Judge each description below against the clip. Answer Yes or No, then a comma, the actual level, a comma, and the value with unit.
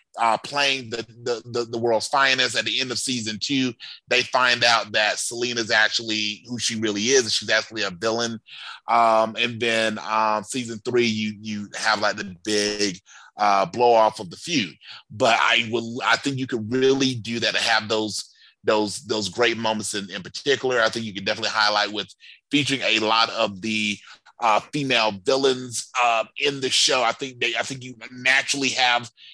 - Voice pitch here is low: Yes, low, 115 Hz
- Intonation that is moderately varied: No, narrow, 2.2 semitones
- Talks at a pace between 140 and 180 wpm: No, average, 190 wpm